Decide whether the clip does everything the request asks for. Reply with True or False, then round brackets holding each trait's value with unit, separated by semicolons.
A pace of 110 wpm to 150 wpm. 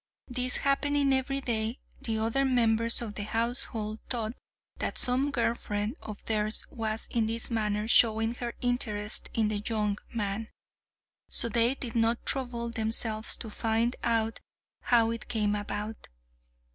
True (145 wpm)